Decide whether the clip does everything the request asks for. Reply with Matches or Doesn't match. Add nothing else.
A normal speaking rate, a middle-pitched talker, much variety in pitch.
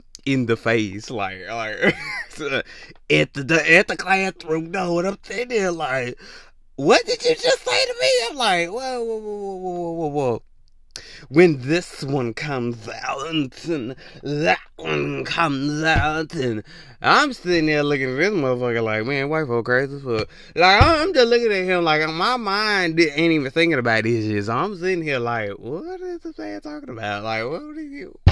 Matches